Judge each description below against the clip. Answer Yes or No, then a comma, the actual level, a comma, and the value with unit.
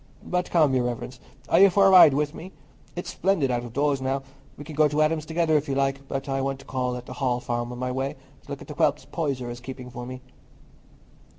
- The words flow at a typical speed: No, fast, 255 wpm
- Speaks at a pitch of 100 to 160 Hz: Yes, low, 135 Hz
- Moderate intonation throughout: Yes, average, 3.4 semitones